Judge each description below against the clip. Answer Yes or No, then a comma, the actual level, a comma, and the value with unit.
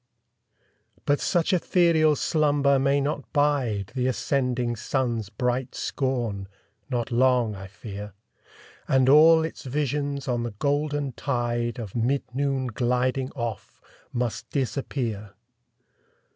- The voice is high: No, low, 130 Hz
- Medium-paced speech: No, slow, 115 wpm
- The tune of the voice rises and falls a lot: No, average, 3.2 semitones